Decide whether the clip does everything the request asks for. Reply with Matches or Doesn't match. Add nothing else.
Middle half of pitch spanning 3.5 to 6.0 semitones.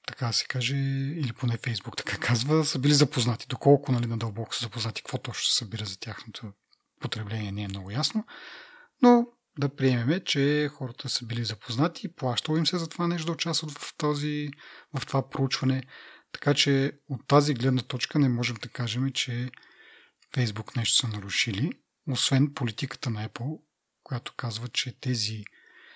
Matches